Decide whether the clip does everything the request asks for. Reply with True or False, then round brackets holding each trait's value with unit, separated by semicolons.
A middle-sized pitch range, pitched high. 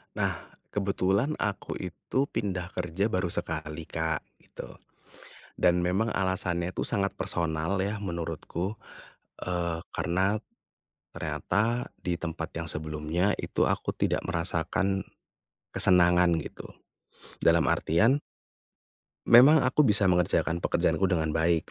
False (3.1 semitones; 90 Hz)